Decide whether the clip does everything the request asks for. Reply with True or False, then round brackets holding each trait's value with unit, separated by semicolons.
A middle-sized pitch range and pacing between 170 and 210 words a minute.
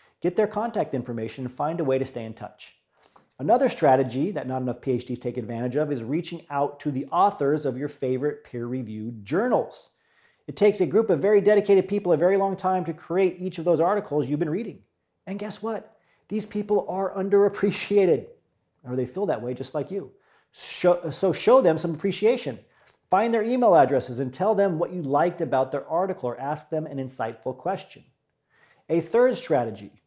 False (7.1 semitones; 190 wpm)